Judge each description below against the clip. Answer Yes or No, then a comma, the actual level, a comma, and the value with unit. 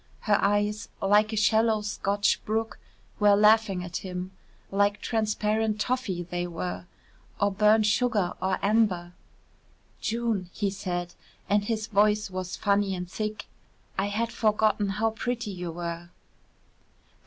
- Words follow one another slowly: Yes, slow, 130 wpm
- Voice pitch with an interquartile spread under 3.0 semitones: Yes, narrow, 2.5 semitones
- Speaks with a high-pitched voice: Yes, high, 205 Hz